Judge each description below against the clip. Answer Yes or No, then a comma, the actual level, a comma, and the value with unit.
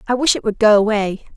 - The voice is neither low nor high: No, high, 215 Hz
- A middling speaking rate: No, fast, 265 wpm